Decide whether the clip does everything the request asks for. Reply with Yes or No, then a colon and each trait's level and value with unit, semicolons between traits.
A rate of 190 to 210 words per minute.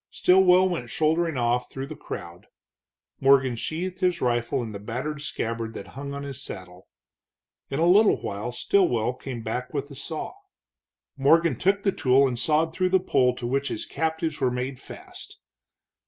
No: average, 170 wpm